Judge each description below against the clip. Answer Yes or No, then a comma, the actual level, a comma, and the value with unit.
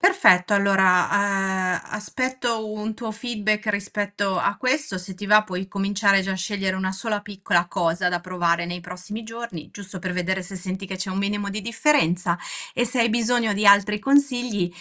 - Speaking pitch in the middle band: No, high, 200 Hz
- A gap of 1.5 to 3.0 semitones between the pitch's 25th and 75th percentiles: Yes, average, 2.7 semitones